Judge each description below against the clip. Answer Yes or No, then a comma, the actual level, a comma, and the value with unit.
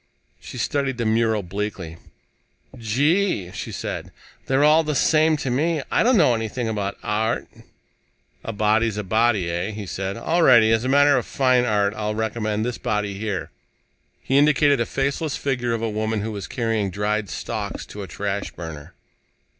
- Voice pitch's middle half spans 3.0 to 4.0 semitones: No, average, 4.4 semitones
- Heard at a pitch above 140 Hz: No, low, 110 Hz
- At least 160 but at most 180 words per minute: Yes, average, 175 wpm